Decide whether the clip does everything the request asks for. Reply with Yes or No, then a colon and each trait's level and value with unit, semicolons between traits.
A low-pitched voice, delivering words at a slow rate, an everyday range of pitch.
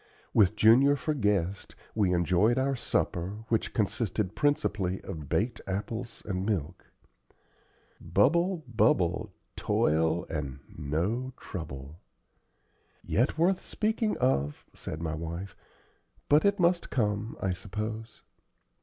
No: low, 105 Hz; slow, 115 wpm; wide, 6.6 semitones